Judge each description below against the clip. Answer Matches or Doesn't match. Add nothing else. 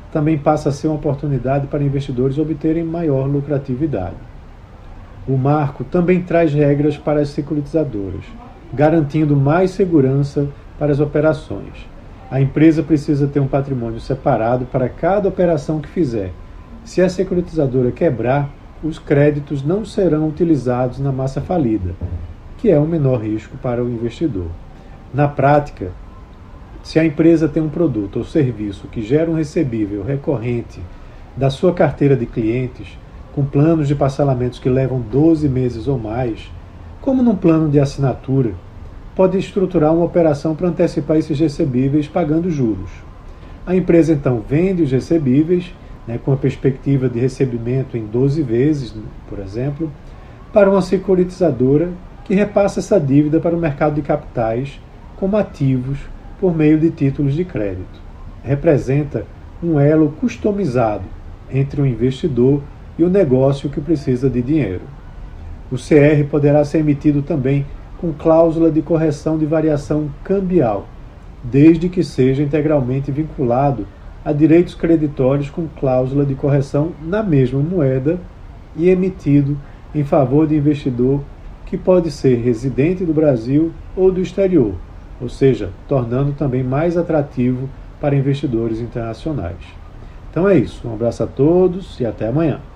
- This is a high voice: Doesn't match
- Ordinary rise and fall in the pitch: Matches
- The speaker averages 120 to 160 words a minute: Matches